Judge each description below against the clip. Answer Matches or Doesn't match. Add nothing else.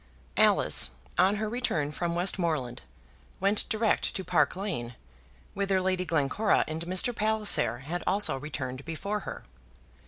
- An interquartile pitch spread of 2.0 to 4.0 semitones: Doesn't match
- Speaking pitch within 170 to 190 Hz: Matches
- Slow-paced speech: Matches